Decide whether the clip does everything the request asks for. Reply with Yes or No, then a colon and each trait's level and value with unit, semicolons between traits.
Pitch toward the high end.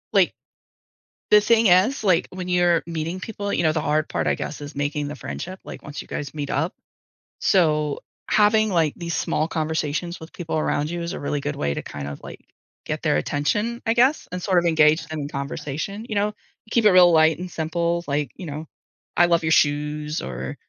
No: medium, 160 Hz